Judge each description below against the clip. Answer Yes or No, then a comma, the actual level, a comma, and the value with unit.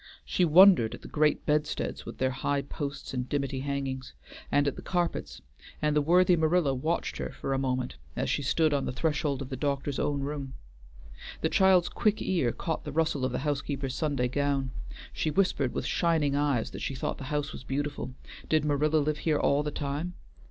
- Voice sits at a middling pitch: Yes, medium, 145 Hz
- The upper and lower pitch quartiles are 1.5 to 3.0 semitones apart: Yes, narrow, 2.5 semitones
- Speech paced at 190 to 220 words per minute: Yes, average, 200 wpm